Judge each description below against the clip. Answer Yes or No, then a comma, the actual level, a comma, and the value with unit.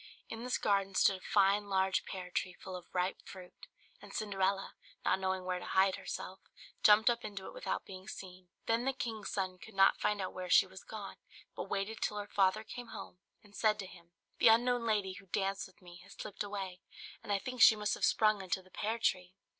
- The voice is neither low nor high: No, high, 195 Hz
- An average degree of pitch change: No, narrow, 2.3 semitones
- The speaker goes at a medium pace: No, fast, 220 wpm